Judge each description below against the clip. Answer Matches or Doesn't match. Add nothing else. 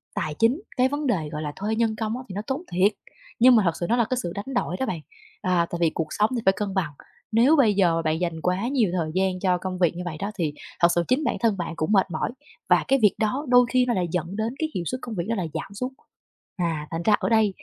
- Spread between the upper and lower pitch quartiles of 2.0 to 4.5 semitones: Doesn't match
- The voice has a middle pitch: Doesn't match